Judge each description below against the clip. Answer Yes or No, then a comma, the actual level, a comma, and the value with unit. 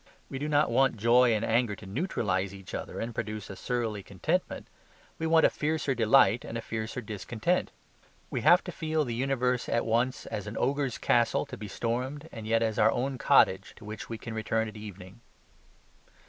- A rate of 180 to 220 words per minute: Yes, average, 195 wpm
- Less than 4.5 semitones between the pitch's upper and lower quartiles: Yes, average, 3.4 semitones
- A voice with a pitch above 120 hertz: No, low, 115 Hz